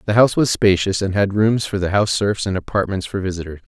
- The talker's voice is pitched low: Yes, low, 100 Hz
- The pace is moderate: No, fast, 240 wpm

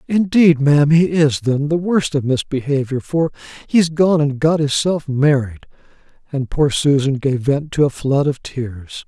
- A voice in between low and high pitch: Yes, medium, 145 Hz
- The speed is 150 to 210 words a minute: Yes, average, 170 wpm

